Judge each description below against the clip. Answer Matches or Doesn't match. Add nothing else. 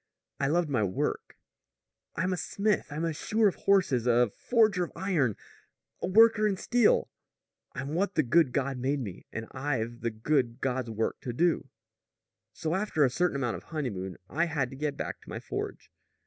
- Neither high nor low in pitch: Matches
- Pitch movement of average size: Doesn't match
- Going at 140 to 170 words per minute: Doesn't match